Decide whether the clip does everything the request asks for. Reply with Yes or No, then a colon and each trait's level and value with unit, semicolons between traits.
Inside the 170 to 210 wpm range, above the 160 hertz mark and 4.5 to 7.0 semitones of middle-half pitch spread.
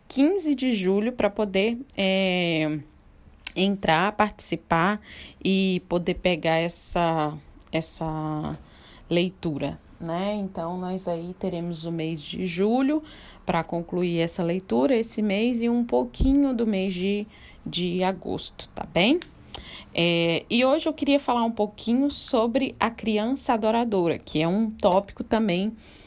No: average, 130 wpm; high, 190 Hz; average, 5.1 semitones